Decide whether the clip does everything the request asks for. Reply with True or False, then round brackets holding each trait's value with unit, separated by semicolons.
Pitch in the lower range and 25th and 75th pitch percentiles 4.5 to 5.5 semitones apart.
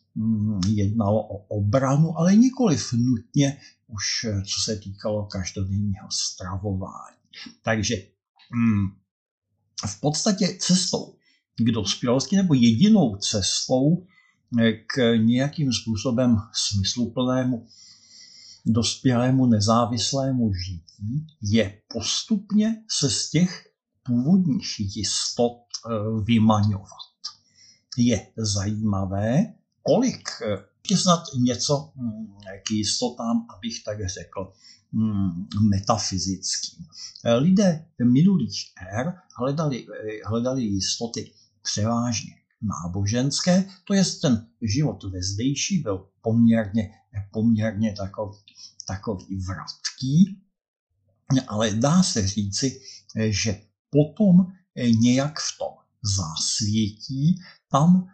True (115 Hz; 5.1 semitones)